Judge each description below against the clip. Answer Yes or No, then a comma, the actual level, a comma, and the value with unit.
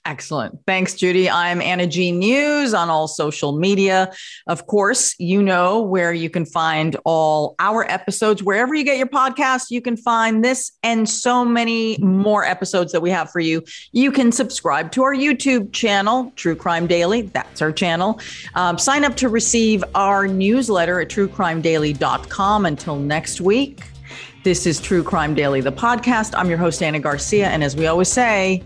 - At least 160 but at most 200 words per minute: Yes, average, 175 wpm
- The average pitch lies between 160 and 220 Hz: Yes, high, 190 Hz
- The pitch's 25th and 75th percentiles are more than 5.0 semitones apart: Yes, wide, 5.4 semitones